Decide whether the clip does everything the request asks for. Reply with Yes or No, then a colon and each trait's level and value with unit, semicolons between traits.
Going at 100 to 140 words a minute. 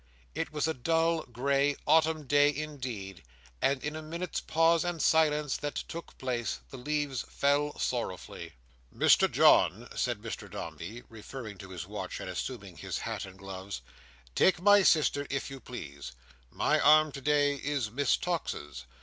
No: average, 155 wpm